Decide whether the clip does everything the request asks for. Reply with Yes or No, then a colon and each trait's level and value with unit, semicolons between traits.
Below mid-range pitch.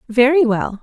No: very high, 250 Hz